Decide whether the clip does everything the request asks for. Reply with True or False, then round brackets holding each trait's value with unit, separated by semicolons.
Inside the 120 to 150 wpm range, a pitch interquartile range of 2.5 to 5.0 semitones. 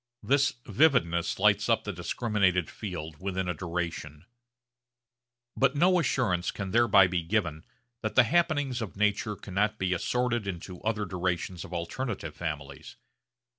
False (135 wpm; 5.4 semitones)